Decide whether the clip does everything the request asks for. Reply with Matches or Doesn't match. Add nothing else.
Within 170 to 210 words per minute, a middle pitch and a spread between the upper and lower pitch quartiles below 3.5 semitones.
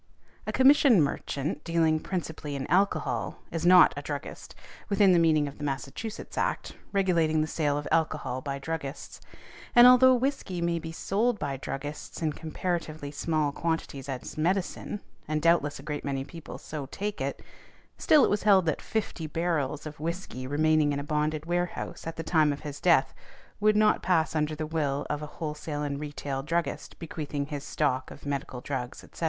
Matches